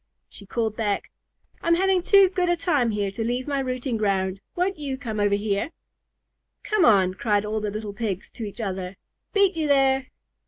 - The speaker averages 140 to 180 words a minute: No, average, 190 wpm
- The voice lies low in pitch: No, high, 230 Hz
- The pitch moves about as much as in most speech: No, wide, 6.6 semitones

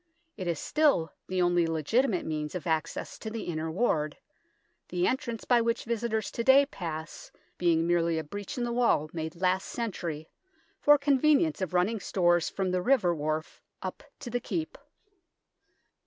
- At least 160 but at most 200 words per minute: Yes, average, 165 wpm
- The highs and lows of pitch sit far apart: Yes, wide, 6.4 semitones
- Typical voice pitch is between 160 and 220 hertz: Yes, medium, 185 Hz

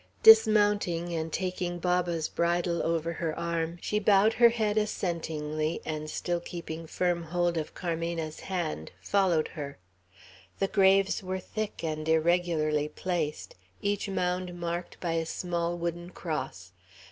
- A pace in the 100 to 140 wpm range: Yes, slow, 135 wpm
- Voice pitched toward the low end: No, medium, 170 Hz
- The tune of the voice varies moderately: No, narrow, 2.3 semitones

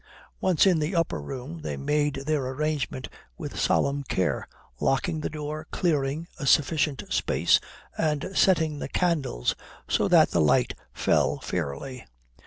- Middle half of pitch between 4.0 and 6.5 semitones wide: No, average, 3.0 semitones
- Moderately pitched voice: Yes, medium, 150 Hz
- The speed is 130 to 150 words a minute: Yes, average, 140 wpm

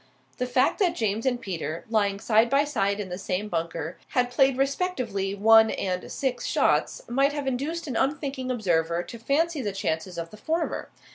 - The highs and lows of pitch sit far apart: Yes, wide, 5.9 semitones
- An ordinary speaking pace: Yes, average, 185 wpm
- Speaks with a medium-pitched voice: No, high, 230 Hz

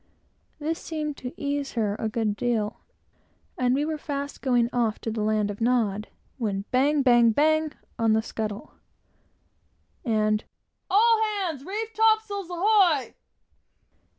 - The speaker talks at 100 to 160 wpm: Yes, slow, 135 wpm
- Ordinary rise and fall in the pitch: No, wide, 6.5 semitones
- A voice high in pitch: Yes, very high, 260 Hz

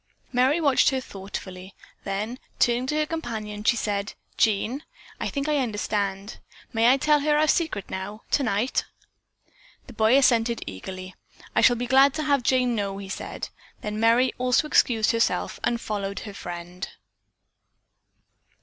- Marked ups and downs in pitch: No, average, 4.6 semitones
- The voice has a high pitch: Yes, high, 230 Hz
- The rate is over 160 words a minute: No, average, 150 wpm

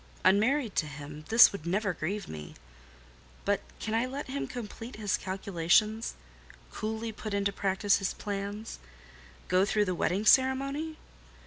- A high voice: Yes, high, 200 Hz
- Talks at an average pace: No, slow, 130 wpm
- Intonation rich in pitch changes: No, average, 4.7 semitones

